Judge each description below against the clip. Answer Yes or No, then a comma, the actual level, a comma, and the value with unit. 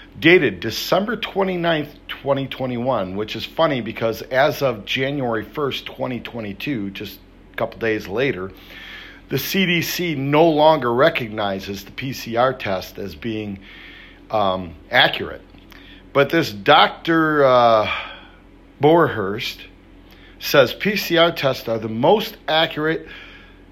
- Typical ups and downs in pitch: No, wide, 7.0 semitones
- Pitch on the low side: Yes, low, 130 Hz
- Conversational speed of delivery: No, slow, 110 wpm